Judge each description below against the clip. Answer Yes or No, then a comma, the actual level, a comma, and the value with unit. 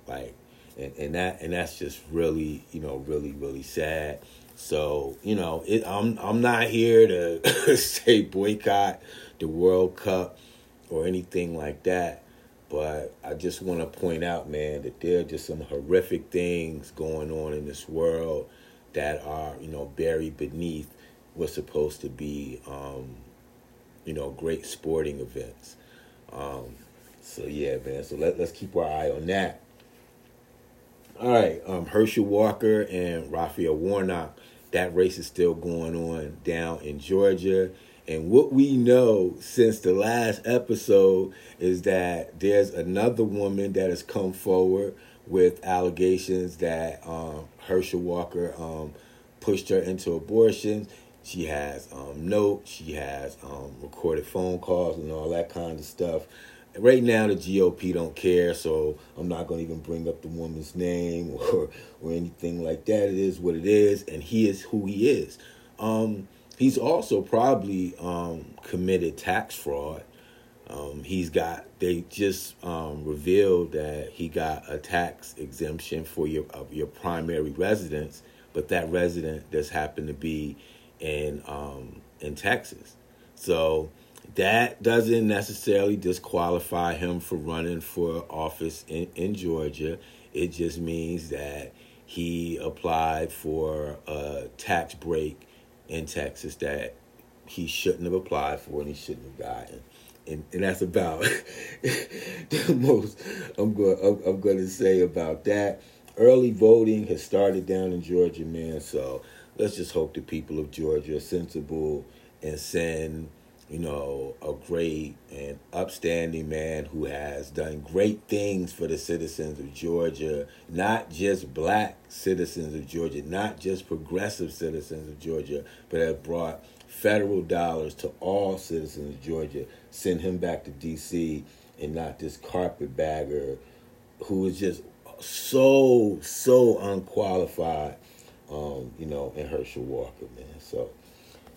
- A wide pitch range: No, average, 3.5 semitones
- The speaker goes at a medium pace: Yes, average, 145 wpm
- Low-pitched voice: Yes, very low, 85 Hz